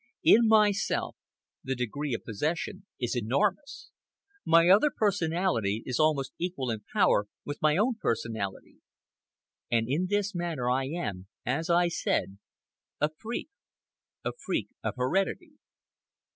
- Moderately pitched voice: Yes, medium, 155 Hz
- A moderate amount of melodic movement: No, wide, 7.6 semitones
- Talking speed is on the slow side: Yes, slow, 125 wpm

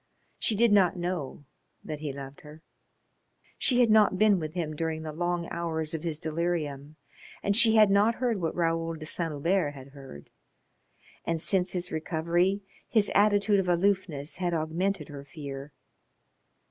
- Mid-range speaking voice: Yes, medium, 170 Hz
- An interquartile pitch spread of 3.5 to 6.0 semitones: Yes, average, 4.2 semitones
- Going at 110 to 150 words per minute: No, average, 160 wpm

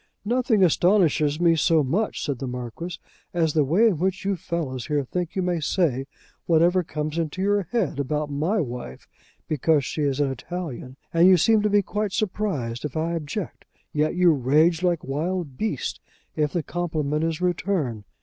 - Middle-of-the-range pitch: Yes, medium, 165 Hz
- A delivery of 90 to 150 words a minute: No, average, 180 wpm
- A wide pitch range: No, average, 3.9 semitones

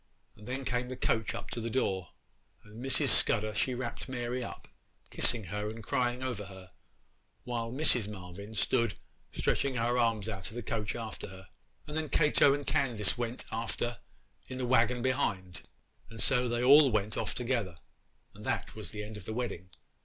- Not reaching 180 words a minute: No, average, 185 wpm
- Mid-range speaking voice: No, low, 115 Hz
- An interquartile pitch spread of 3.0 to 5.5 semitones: Yes, average, 3.3 semitones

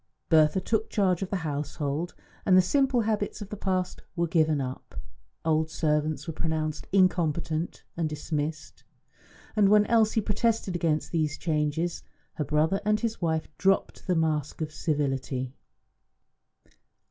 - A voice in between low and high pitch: Yes, medium, 165 Hz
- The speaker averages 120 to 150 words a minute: Yes, average, 140 wpm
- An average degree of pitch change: Yes, average, 4.2 semitones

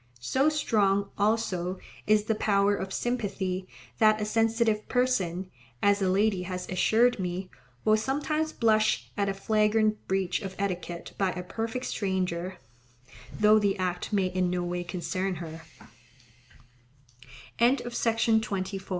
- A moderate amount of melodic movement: Yes, average, 3.1 semitones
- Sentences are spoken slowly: Yes, slow, 130 wpm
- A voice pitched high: Yes, high, 200 Hz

